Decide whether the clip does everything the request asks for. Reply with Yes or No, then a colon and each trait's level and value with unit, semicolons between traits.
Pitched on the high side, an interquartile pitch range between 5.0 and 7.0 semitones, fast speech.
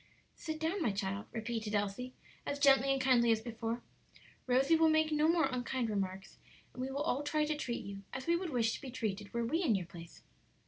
Yes: very high, 250 Hz; average, 5.3 semitones; fast, 220 wpm